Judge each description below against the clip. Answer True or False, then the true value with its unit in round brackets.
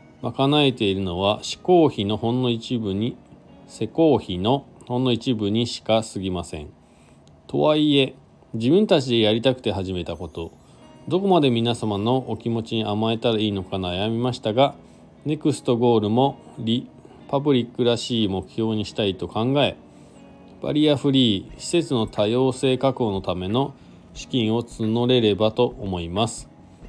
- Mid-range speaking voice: False (115 Hz)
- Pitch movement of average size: True (4.2 semitones)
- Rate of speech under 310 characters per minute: True (300 characters per minute)